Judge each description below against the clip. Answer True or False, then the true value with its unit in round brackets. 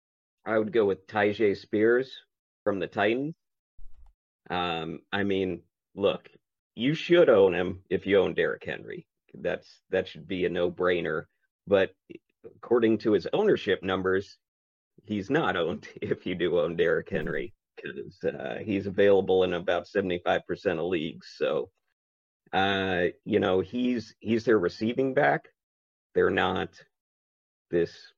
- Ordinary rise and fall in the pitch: False (7.8 semitones)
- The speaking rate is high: False (135 wpm)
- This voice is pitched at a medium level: False (105 Hz)